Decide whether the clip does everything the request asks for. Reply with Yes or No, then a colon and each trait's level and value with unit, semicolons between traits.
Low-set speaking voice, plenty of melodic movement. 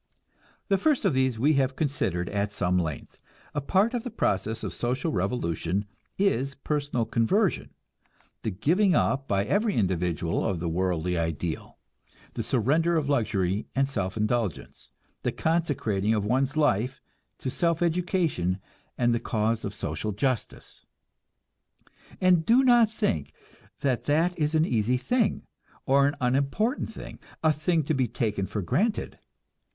Yes: low, 130 Hz; wide, 8.1 semitones